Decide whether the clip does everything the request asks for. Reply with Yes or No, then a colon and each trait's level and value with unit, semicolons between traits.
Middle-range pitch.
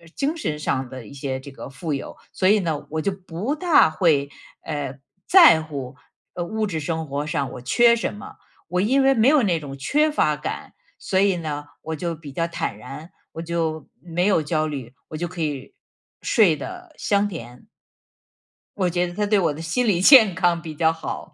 Yes: medium, 165 Hz